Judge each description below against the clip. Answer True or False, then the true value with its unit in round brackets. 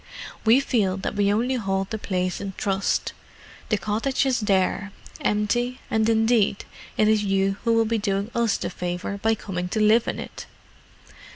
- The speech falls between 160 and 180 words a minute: True (175 wpm)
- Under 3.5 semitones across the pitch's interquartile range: True (2.6 semitones)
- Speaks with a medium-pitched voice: False (210 Hz)